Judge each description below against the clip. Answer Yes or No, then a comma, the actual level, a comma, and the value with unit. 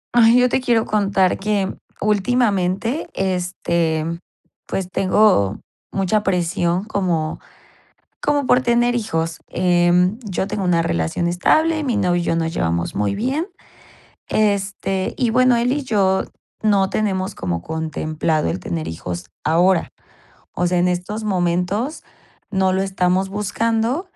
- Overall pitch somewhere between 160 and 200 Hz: Yes, high, 190 Hz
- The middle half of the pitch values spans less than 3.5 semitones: No, average, 4.0 semitones